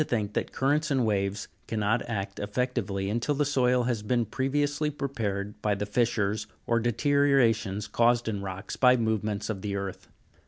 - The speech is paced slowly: No, average, 160 wpm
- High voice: No, low, 115 Hz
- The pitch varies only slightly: No, average, 3.8 semitones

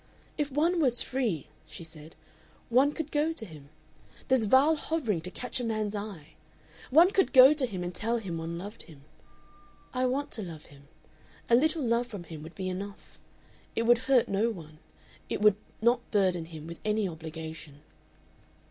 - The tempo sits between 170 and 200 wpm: Yes, average, 180 wpm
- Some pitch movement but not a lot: No, wide, 7.5 semitones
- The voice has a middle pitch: No, high, 210 Hz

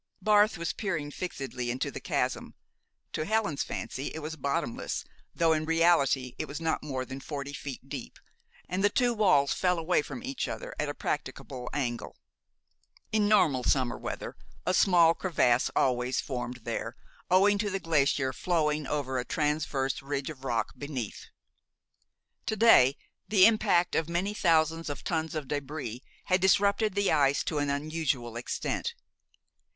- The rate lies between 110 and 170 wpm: Yes, average, 155 wpm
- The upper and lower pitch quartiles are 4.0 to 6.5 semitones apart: Yes, average, 5.2 semitones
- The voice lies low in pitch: No, medium, 155 Hz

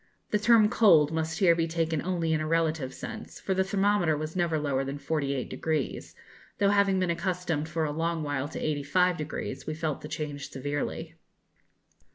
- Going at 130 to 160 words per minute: No, average, 175 wpm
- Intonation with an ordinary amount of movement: Yes, average, 3.3 semitones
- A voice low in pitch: No, medium, 160 Hz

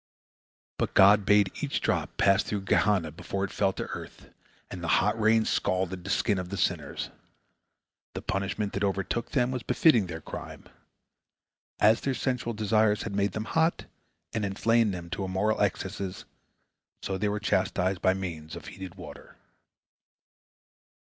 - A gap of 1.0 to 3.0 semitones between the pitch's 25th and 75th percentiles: Yes, narrow, 2.5 semitones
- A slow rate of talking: No, average, 155 wpm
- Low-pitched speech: Yes, low, 100 Hz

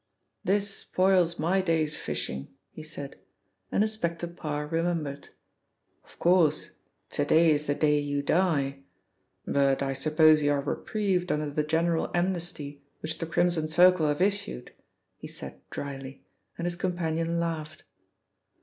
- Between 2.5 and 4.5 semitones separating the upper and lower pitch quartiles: Yes, average, 3.1 semitones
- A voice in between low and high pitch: Yes, medium, 160 Hz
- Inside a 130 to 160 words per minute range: Yes, average, 140 wpm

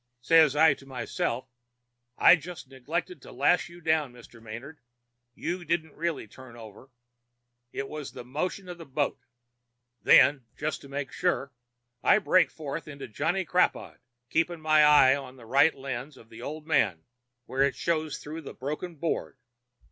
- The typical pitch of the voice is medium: Yes, medium, 145 Hz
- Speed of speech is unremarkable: Yes, average, 165 wpm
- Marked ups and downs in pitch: No, average, 3.7 semitones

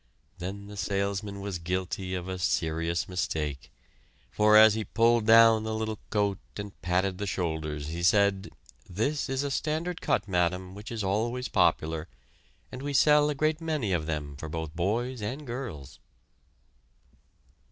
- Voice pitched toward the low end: Yes, low, 100 Hz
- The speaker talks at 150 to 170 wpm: Yes, average, 155 wpm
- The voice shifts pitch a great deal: No, average, 4.6 semitones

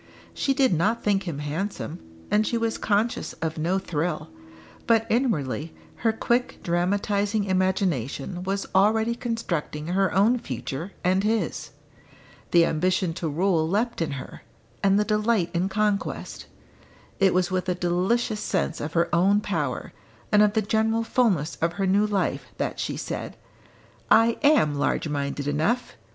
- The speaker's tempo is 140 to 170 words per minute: Yes, average, 150 wpm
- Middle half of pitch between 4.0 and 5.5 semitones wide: Yes, average, 4.5 semitones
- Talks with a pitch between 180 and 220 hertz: Yes, high, 190 Hz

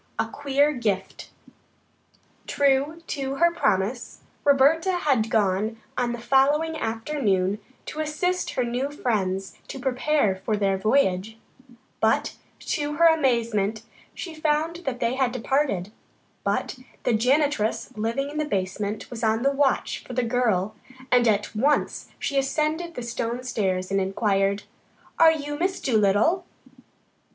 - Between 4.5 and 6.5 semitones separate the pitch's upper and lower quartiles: Yes, wide, 5.6 semitones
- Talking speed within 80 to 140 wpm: Yes, slow, 135 wpm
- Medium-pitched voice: No, very high, 250 Hz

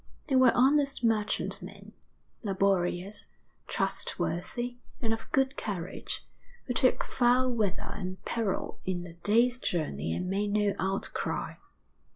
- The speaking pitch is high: Yes, high, 210 Hz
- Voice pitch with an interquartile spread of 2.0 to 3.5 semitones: No, average, 4.7 semitones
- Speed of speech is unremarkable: No, slow, 120 wpm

